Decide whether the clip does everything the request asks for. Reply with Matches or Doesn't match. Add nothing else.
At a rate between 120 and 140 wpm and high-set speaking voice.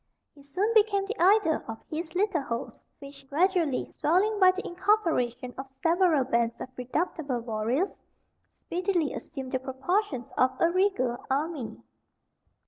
Matches